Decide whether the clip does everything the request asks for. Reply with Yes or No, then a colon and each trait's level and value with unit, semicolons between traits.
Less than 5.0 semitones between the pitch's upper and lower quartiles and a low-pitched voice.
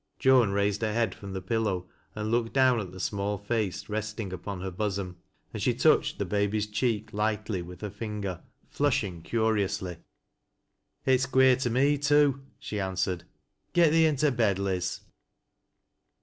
Yes: average, 3.9 semitones; low, 105 Hz